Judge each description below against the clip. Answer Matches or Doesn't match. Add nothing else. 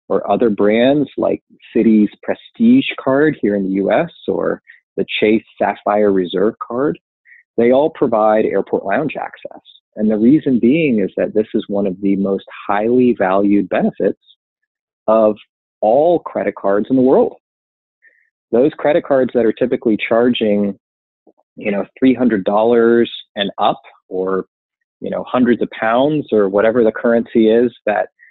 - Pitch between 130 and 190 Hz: Doesn't match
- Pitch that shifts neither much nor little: Matches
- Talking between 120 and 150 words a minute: Matches